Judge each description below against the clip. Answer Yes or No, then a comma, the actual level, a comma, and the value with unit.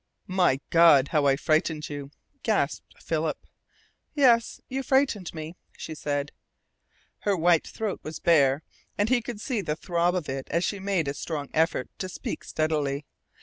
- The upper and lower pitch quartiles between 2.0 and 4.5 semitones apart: No, average, 5.2 semitones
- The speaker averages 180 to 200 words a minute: No, average, 160 wpm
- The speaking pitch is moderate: Yes, medium, 165 Hz